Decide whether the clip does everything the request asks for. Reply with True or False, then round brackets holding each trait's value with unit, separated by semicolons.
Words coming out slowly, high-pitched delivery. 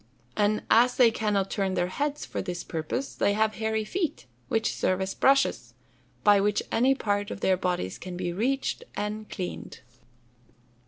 False (165 wpm; 210 Hz)